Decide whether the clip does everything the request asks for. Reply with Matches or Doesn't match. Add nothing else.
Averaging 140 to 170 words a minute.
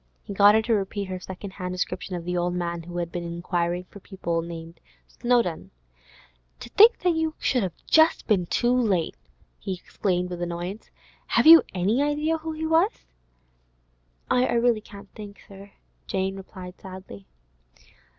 Matches